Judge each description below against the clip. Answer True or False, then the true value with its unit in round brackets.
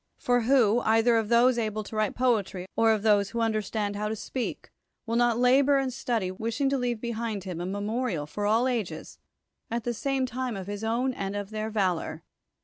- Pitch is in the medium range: False (225 Hz)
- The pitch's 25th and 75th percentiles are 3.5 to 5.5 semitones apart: False (3.0 semitones)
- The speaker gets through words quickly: True (210 wpm)